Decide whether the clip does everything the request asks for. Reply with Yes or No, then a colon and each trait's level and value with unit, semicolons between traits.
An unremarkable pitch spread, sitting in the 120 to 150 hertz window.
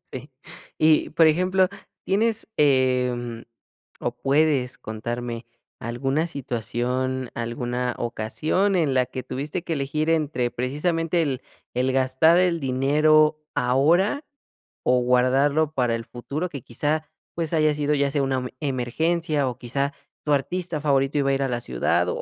Yes: average, 3.8 semitones; medium, 140 Hz